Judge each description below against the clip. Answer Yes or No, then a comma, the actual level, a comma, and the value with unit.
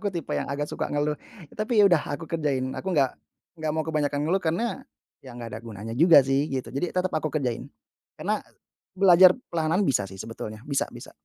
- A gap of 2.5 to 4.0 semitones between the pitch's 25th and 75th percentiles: No, average, 4.7 semitones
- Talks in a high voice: No, medium, 150 Hz